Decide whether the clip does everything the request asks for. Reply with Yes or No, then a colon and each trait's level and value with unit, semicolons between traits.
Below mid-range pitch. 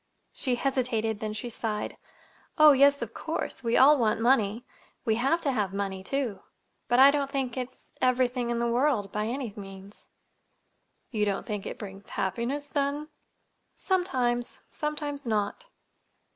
No: high, 245 Hz